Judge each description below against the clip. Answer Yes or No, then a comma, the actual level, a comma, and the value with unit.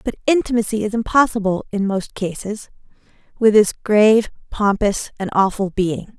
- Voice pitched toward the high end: Yes, high, 210 Hz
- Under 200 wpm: Yes, slow, 135 wpm